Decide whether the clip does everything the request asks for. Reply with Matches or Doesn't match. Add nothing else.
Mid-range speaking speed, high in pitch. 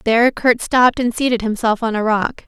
Doesn't match